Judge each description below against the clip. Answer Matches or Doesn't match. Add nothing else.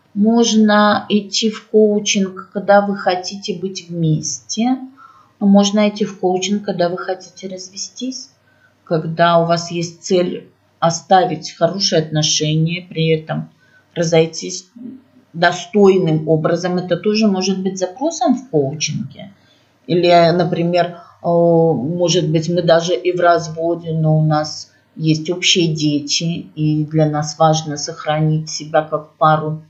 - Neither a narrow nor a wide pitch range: Matches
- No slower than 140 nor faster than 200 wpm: Doesn't match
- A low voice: Doesn't match